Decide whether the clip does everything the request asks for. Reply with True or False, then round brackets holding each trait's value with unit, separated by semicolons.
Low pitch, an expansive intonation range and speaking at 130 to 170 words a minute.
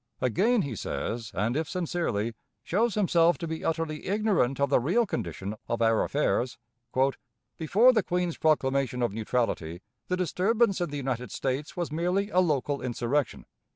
False (150 Hz; 6.8 semitones; 155 wpm)